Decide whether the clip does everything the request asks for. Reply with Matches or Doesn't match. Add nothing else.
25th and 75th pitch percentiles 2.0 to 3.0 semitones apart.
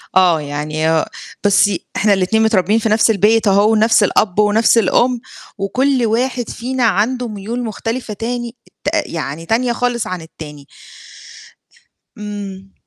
Doesn't match